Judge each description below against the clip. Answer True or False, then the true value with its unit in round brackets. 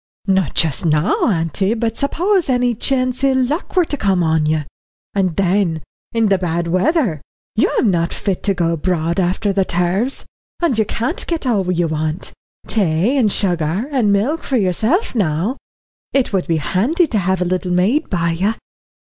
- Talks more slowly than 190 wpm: True (175 wpm)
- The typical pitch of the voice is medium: False (195 Hz)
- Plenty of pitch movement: True (6.2 semitones)